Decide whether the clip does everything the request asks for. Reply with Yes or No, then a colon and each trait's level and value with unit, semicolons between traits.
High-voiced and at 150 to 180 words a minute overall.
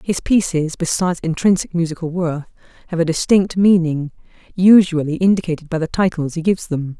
No: medium, 170 Hz; average, 155 wpm